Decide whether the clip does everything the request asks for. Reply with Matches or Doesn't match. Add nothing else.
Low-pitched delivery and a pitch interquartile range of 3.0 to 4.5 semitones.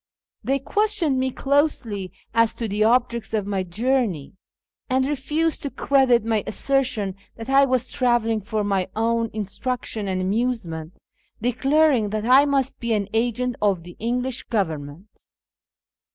Doesn't match